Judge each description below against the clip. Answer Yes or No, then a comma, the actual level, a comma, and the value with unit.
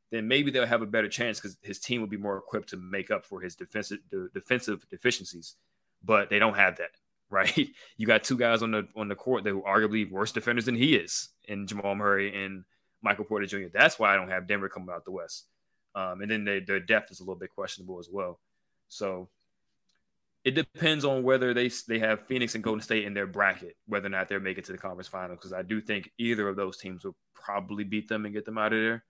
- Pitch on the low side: Yes, low, 105 Hz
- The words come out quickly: Yes, fast, 245 wpm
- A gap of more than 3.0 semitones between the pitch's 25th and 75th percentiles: No, average, 2.7 semitones